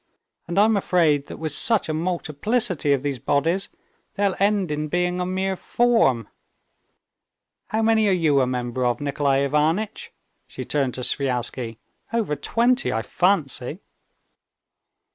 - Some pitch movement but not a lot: No, wide, 6.0 semitones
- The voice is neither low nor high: Yes, medium, 160 Hz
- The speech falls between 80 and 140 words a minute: Yes, slow, 135 wpm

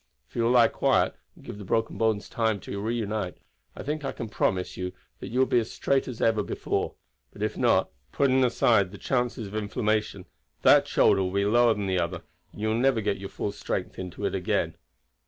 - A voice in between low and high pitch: No, low, 110 Hz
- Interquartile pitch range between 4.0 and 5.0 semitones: No, average, 3.2 semitones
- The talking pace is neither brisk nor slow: No, fast, 215 wpm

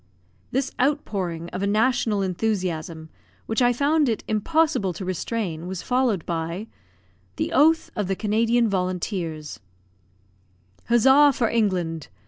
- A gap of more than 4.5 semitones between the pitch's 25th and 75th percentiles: Yes, average, 5.3 semitones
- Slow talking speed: Yes, slow, 120 wpm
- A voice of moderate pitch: No, high, 210 Hz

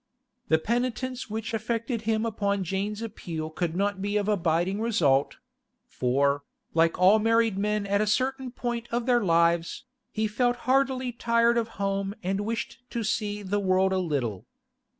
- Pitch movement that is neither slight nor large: Yes, average, 3.8 semitones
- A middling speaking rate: Yes, average, 160 wpm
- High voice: Yes, high, 210 Hz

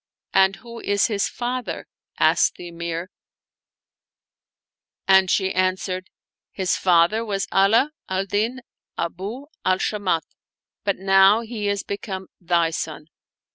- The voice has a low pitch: No, high, 195 Hz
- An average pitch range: No, narrow, 2.3 semitones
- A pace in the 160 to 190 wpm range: No, slow, 135 wpm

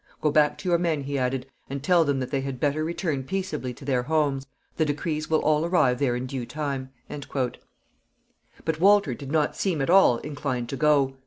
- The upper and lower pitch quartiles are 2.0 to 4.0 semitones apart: Yes, average, 2.8 semitones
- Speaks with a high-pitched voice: No, medium, 145 Hz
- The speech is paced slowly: No, average, 200 wpm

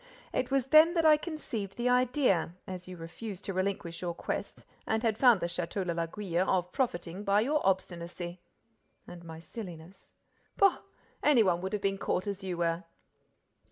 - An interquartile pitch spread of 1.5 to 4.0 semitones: No, average, 5.2 semitones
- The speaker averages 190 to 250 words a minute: No, average, 175 wpm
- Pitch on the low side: No, high, 190 Hz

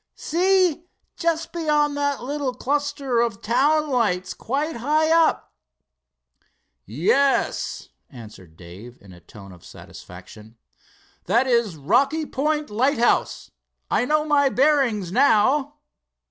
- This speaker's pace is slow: Yes, slow, 110 wpm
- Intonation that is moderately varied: No, wide, 7.5 semitones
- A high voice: Yes, very high, 270 Hz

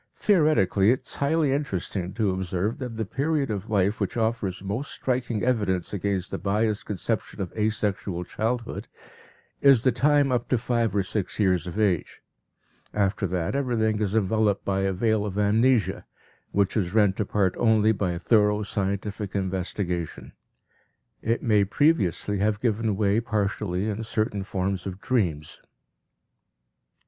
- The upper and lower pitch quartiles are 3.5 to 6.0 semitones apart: No, average, 3.0 semitones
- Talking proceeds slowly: No, average, 145 wpm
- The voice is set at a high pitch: No, low, 105 Hz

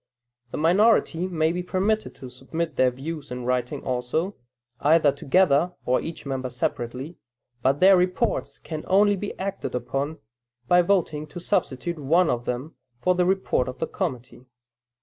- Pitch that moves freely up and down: Yes, wide, 5.8 semitones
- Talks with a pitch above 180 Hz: No, medium, 160 Hz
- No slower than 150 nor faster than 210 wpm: Yes, average, 155 wpm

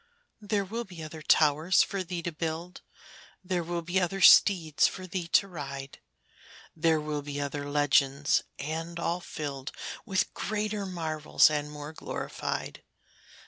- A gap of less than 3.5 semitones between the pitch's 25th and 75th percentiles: No, average, 3.8 semitones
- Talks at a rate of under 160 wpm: Yes, average, 140 wpm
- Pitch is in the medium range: Yes, medium, 165 Hz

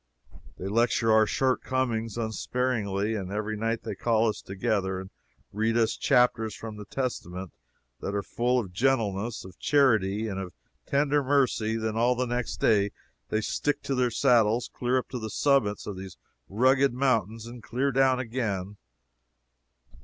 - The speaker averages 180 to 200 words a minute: No, average, 165 wpm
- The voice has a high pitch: No, low, 115 Hz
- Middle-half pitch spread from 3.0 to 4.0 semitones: Yes, average, 3.4 semitones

